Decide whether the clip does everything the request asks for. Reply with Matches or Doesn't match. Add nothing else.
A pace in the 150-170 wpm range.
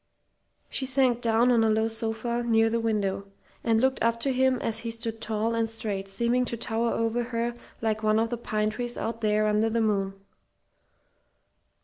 Doesn't match